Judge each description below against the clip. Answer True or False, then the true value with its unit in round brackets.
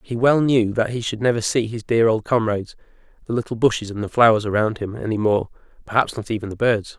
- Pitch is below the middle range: True (115 Hz)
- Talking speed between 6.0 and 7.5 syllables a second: True (6.1 syllables/s)